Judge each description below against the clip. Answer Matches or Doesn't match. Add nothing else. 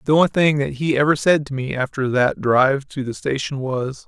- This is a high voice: Doesn't match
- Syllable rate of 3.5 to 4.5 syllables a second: Doesn't match